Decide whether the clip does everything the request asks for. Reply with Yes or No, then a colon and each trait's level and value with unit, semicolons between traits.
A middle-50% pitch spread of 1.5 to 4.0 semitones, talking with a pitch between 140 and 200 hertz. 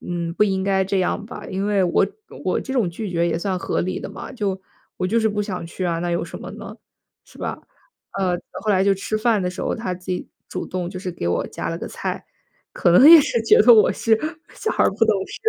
Yes: average, 3.0 semitones; high, 190 Hz